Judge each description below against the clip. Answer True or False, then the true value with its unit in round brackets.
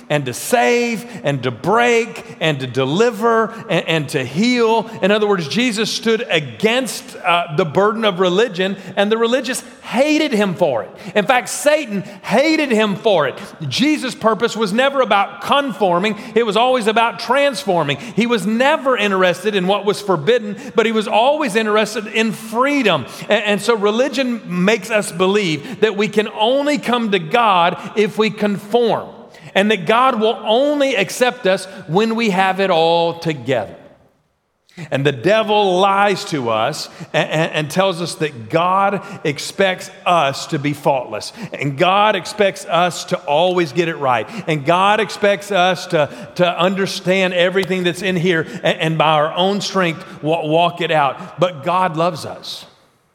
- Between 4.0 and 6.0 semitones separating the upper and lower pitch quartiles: True (4.5 semitones)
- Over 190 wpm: False (165 wpm)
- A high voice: True (200 Hz)